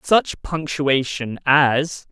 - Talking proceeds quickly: No, slow, 85 wpm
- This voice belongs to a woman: No, male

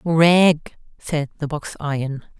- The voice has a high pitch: No, medium, 155 Hz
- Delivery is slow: Yes, slow, 125 wpm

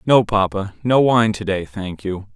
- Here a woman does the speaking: No, male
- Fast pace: No, average, 180 wpm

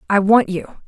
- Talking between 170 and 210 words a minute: Yes, fast, 205 wpm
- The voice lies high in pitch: Yes, high, 205 Hz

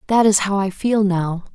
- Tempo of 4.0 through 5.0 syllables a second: Yes, 4.7 syllables/s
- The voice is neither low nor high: No, high, 200 Hz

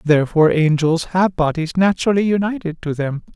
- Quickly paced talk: No, average, 145 wpm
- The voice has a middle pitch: Yes, medium, 170 Hz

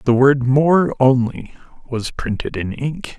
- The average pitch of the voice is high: No, low, 130 Hz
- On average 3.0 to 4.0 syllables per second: Yes, 3.6 syllables/s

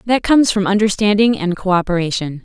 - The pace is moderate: Yes, average, 150 wpm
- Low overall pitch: No, high, 200 Hz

